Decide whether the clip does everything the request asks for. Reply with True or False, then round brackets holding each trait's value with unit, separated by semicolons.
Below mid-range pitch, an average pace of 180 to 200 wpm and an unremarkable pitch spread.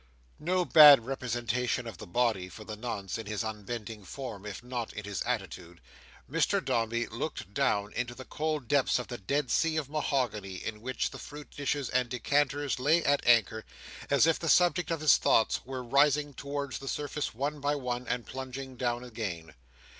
True (125 Hz; 185 wpm; 4.3 semitones)